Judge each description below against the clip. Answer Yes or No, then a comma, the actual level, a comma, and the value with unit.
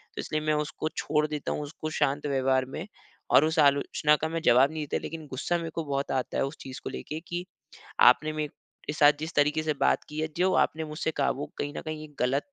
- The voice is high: No, medium, 150 Hz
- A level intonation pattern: Yes, narrow, 1.9 semitones